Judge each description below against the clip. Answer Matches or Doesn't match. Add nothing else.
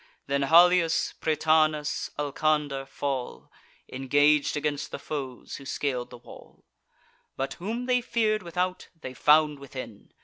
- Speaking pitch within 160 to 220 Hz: Doesn't match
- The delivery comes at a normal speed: Doesn't match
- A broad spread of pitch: Doesn't match